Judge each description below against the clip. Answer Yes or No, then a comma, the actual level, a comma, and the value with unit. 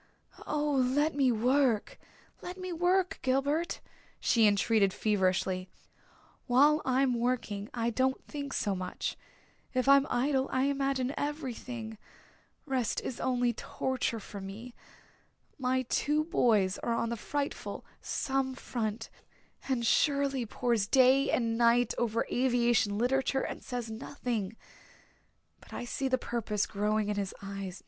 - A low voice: No, high, 245 Hz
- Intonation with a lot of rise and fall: No, average, 3.6 semitones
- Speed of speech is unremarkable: No, slow, 130 wpm